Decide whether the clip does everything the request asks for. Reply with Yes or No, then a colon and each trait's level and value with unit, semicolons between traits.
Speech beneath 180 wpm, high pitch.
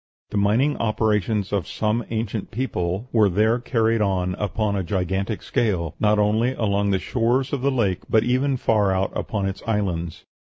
No: average, 170 wpm; low, 105 Hz